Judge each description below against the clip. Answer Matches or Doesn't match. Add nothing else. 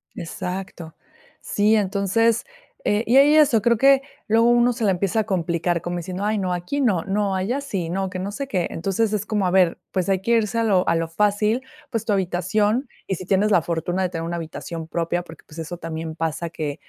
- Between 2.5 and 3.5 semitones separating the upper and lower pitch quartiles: Doesn't match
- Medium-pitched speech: Doesn't match